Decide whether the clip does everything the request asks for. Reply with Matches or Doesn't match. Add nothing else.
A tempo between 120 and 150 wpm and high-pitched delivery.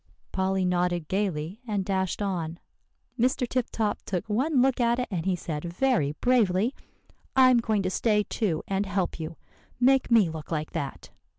Doesn't match